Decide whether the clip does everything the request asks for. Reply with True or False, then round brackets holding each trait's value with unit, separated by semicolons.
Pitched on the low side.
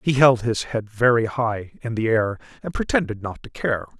True (115 Hz)